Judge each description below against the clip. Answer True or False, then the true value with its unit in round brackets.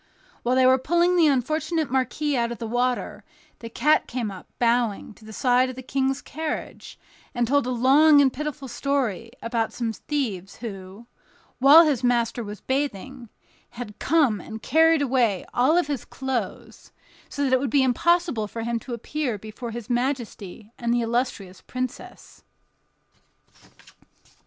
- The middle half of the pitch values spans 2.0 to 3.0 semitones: False (3.5 semitones)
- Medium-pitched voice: False (250 Hz)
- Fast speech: False (155 wpm)